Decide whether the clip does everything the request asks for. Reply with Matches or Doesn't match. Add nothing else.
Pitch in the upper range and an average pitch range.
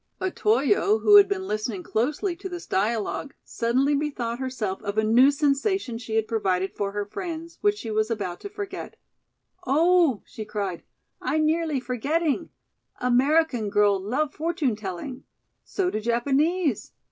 Doesn't match